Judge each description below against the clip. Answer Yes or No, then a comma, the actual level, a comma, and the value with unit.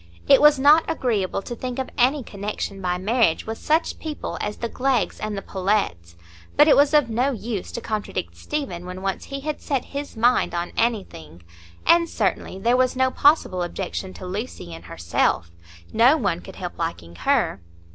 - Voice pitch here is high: Yes, high, 215 Hz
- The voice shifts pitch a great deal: Yes, wide, 6.6 semitones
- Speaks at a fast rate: No, average, 180 wpm